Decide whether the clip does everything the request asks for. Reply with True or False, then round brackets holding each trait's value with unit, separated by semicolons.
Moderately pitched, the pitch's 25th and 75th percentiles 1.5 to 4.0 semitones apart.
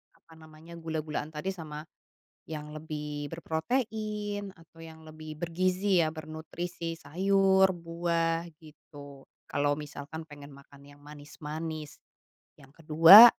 True (160 Hz; 2.5 semitones)